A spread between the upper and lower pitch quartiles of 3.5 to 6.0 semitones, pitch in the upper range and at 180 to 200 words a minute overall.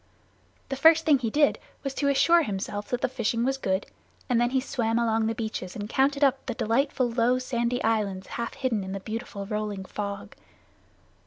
Yes: average, 3.9 semitones; high, 235 Hz; average, 190 wpm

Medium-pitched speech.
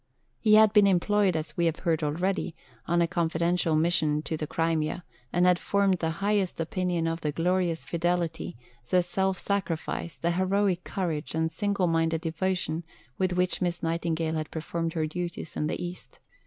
Yes: medium, 170 Hz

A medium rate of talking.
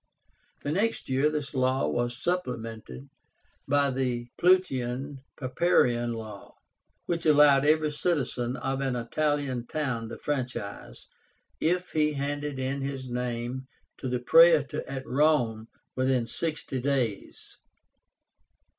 No: slow, 115 wpm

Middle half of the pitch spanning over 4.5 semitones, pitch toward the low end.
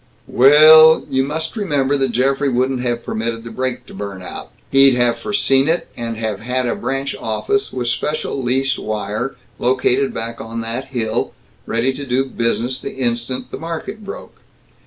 No: average, 2.8 semitones; low, 130 Hz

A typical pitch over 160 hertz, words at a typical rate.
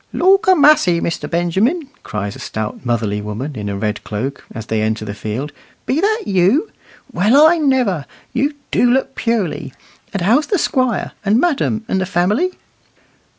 Yes: high, 190 Hz; average, 170 wpm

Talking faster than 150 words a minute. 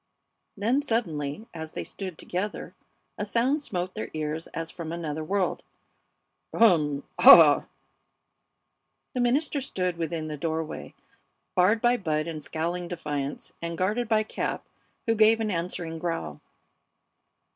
No: slow, 135 wpm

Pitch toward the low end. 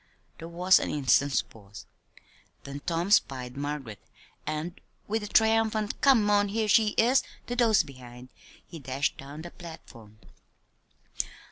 No: medium, 165 Hz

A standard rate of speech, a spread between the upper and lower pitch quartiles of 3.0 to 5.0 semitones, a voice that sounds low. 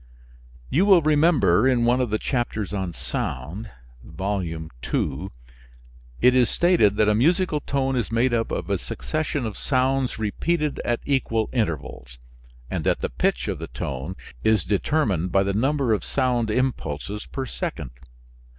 No: average, 155 wpm; wide, 5.6 semitones; low, 115 Hz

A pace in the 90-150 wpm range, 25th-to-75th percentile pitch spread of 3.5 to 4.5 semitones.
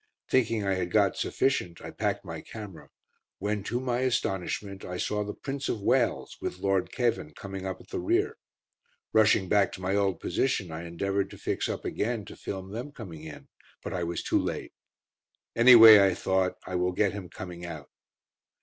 No: average, 185 wpm; average, 3.8 semitones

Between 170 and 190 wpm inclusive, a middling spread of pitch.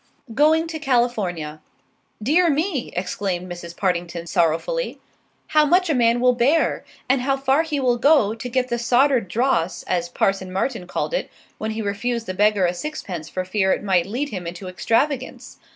No: average, 175 wpm; wide, 6.9 semitones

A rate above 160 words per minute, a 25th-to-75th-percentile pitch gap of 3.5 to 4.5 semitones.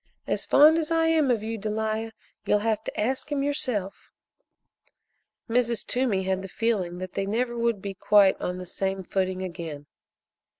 Yes: average, 170 wpm; average, 4.0 semitones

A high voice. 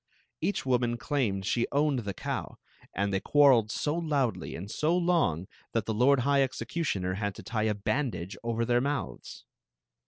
No: low, 120 Hz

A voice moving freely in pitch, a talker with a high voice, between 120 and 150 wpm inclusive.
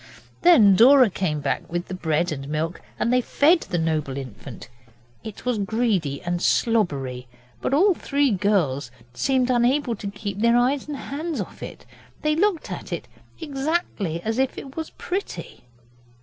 No: wide, 8.9 semitones; high, 220 Hz; average, 165 wpm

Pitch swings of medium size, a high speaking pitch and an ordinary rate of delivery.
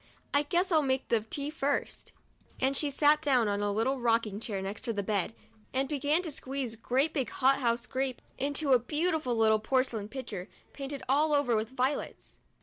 Yes: average, 4.0 semitones; very high, 260 Hz; average, 195 wpm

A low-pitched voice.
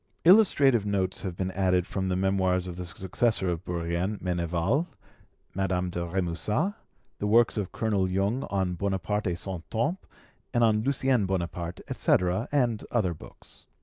Yes: very low, 95 Hz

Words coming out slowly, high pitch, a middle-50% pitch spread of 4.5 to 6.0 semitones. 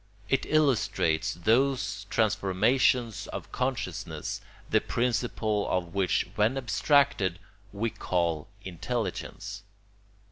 No: slow, 85 wpm; low, 110 Hz; average, 5.1 semitones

